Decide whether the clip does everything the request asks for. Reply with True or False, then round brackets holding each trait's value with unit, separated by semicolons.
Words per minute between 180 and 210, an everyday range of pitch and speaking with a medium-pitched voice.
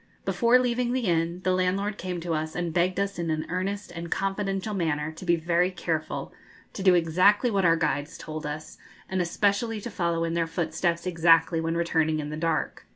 True (200 wpm; 3.0 semitones; 175 Hz)